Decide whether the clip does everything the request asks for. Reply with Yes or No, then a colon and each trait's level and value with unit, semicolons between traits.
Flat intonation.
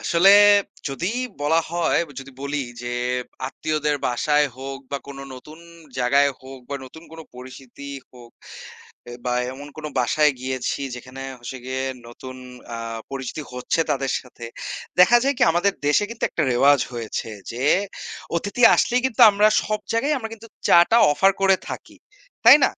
No: average, 4.9 semitones